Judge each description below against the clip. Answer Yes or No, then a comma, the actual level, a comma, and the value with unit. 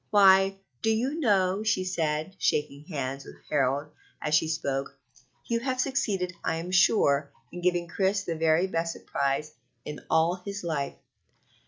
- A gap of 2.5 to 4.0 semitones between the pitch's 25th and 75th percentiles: No, average, 4.4 semitones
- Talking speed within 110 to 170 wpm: Yes, average, 155 wpm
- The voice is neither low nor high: Yes, medium, 175 Hz